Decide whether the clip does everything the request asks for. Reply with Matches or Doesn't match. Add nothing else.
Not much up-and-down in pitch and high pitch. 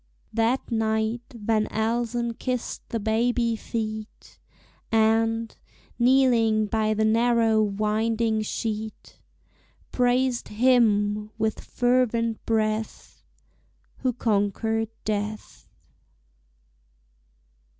Matches